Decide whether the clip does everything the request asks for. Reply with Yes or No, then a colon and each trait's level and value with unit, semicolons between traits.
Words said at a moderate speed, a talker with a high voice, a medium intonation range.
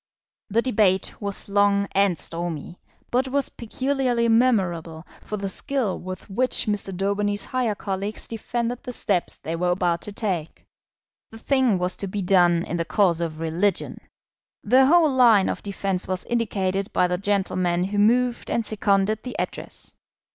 Yes: average, 160 wpm; high, 200 Hz; average, 4.2 semitones